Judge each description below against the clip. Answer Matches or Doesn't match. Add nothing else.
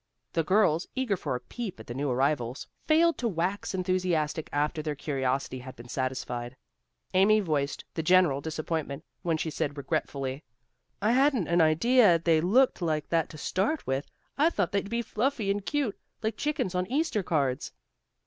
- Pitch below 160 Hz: Doesn't match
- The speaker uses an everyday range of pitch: Doesn't match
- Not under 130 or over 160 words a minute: Doesn't match